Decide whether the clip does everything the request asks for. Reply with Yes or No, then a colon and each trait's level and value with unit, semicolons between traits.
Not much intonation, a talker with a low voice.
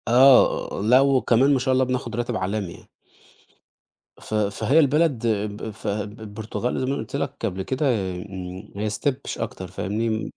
No: average, 4.0 semitones; low, 110 Hz